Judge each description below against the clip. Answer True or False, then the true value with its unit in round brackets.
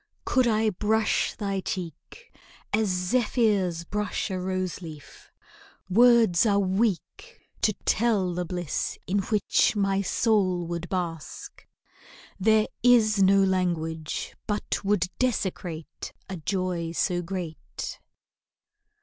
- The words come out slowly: True (110 wpm)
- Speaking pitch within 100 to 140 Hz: False (190 Hz)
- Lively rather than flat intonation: False (3.4 semitones)